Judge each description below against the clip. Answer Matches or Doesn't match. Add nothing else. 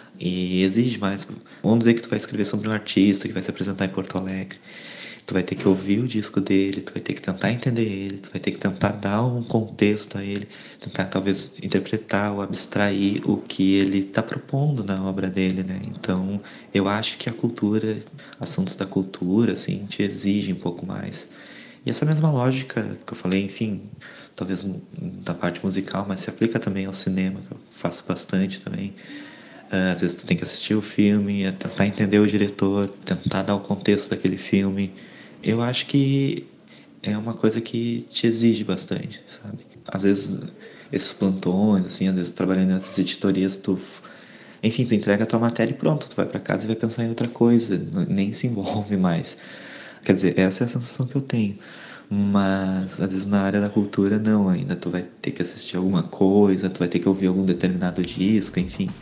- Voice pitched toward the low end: Matches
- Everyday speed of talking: Doesn't match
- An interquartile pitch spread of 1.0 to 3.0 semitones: Matches